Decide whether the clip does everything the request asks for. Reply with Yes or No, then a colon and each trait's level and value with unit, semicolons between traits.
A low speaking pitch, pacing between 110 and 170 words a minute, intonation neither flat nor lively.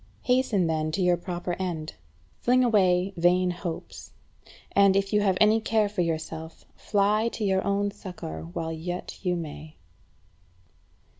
No: medium, 185 Hz; average, 145 wpm; average, 3.4 semitones